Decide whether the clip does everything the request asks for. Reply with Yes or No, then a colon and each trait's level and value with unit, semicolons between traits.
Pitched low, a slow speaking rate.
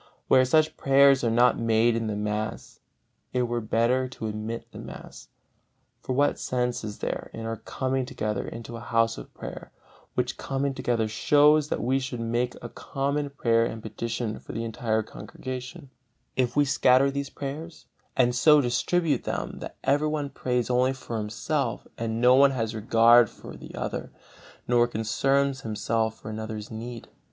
No: low, 120 Hz; average, 165 wpm